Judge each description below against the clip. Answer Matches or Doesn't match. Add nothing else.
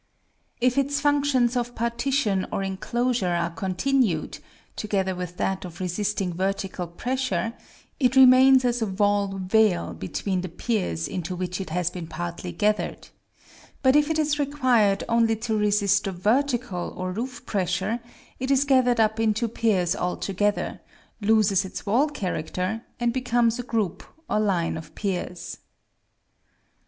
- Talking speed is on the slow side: Doesn't match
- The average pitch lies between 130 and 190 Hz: Doesn't match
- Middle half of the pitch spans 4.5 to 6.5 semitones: Matches